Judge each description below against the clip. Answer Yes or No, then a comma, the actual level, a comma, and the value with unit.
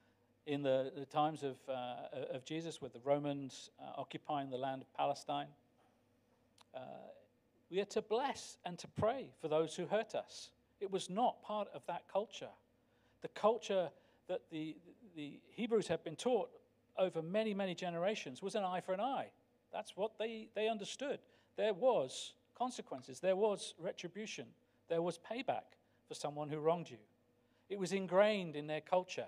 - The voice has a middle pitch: Yes, medium, 175 Hz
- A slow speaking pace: No, average, 165 wpm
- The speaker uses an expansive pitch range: Yes, wide, 6.7 semitones